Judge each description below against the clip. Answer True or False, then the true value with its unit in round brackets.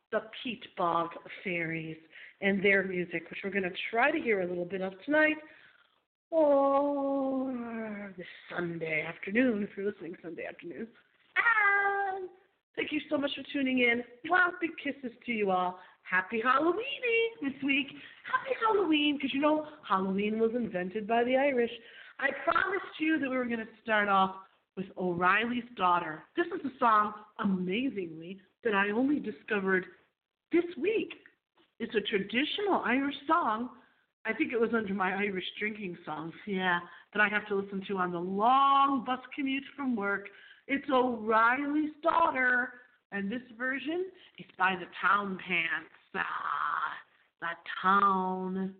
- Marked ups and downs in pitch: True (6.8 semitones)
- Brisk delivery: False (150 wpm)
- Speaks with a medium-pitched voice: False (230 Hz)